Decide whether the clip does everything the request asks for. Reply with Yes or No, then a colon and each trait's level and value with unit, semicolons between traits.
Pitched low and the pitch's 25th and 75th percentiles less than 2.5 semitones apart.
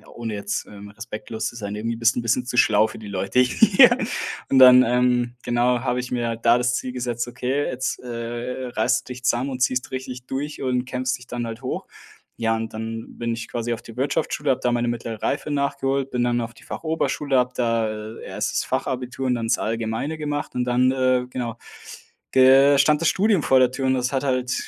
Yes: low, 125 Hz; narrow, 2.0 semitones